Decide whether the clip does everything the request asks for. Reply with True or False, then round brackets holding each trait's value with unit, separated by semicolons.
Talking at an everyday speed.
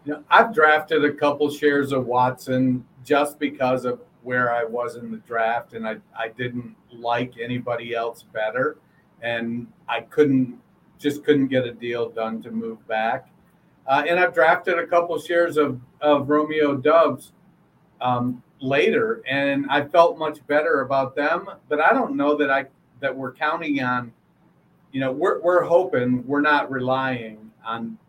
True (165 wpm)